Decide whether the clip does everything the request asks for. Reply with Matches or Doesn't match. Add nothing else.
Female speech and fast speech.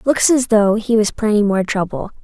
Matches